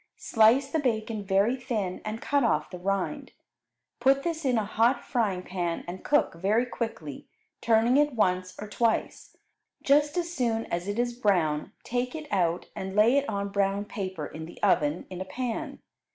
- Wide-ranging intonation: No, average, 4.9 semitones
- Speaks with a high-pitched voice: Yes, high, 215 Hz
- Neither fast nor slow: Yes, average, 180 wpm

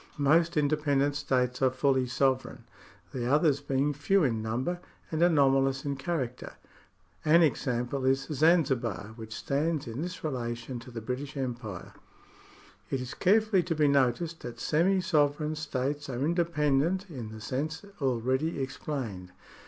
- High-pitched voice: No, medium, 140 Hz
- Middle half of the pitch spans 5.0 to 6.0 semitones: No, average, 3.6 semitones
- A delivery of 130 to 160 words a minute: Yes, average, 145 wpm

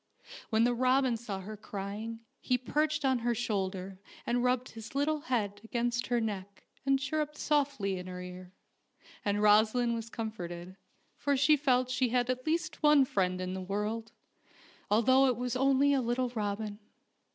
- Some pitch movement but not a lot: Yes, average, 4.1 semitones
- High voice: Yes, high, 235 Hz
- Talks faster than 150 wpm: Yes, average, 165 wpm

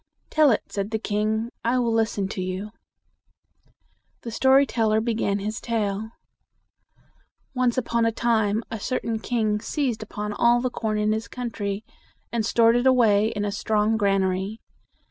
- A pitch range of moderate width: No, narrow, 2.2 semitones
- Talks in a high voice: Yes, high, 220 Hz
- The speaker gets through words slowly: No, average, 165 wpm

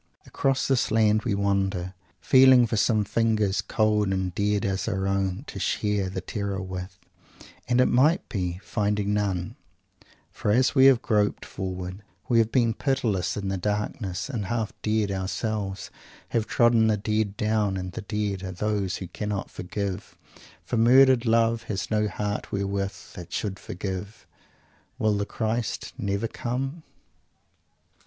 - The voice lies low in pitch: Yes, low, 105 Hz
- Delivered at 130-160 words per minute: Yes, average, 150 wpm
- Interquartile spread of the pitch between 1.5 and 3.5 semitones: Yes, average, 2.7 semitones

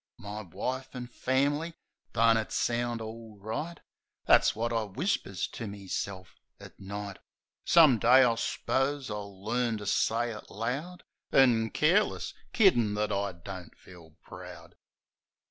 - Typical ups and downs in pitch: Yes, average, 4.3 semitones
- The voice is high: No, low, 115 Hz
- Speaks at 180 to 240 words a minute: No, average, 140 wpm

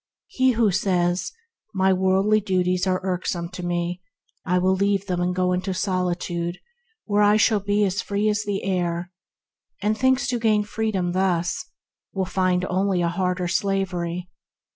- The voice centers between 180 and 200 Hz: Yes, medium, 185 Hz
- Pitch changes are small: Yes, narrow, 2.2 semitones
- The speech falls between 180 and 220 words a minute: No, average, 155 wpm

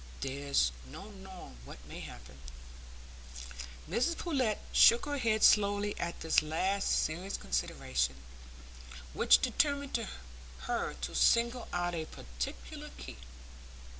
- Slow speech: Yes, slow, 110 wpm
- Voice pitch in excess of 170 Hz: Yes, medium, 185 Hz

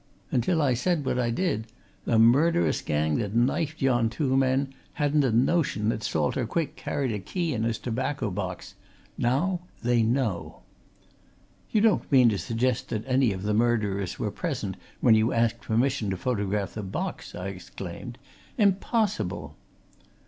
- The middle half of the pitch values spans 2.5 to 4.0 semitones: No, average, 4.6 semitones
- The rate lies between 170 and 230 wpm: No, average, 155 wpm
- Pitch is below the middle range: Yes, low, 120 Hz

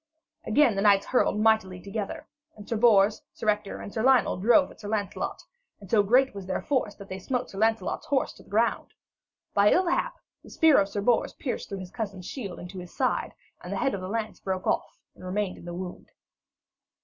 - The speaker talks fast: Yes, fast, 220 wpm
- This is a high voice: Yes, high, 205 Hz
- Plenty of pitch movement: No, average, 3.0 semitones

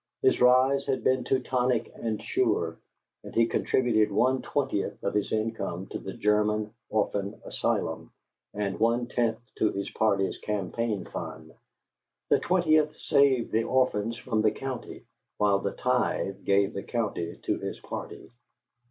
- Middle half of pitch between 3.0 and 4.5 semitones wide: Yes, average, 3.8 semitones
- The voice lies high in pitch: No, low, 110 Hz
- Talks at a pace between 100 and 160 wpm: Yes, average, 145 wpm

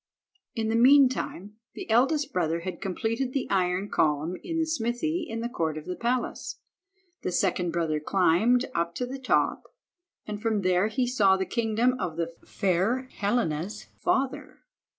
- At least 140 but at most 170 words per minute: Yes, average, 160 wpm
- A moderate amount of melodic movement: No, wide, 5.8 semitones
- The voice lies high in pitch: Yes, high, 215 Hz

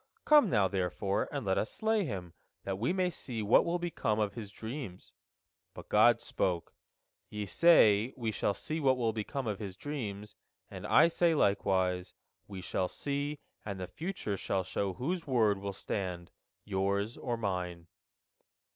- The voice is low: Yes, low, 105 Hz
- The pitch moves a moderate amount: No, wide, 6.3 semitones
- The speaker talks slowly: No, average, 165 wpm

